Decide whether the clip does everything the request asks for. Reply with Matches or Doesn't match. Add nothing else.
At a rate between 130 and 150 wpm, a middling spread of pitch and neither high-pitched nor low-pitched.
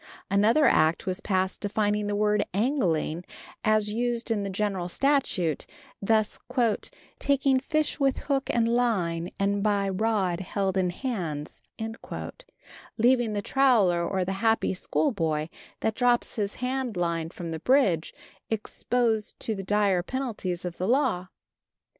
Doesn't match